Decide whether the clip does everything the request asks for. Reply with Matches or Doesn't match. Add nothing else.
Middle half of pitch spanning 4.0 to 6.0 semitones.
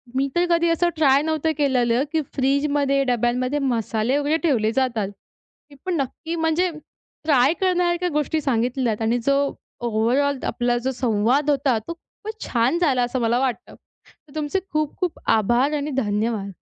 Matches